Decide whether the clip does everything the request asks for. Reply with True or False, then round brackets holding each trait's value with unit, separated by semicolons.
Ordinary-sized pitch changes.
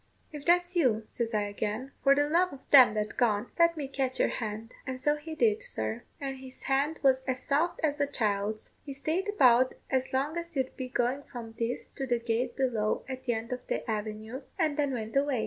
True (4.1 semitones)